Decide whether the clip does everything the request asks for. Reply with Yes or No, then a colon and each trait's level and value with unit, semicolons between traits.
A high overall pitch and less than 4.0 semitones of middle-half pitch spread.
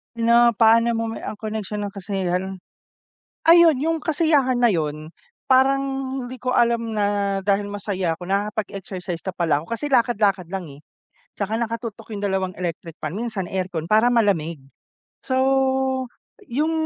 No: high, 210 Hz; average, 4.3 semitones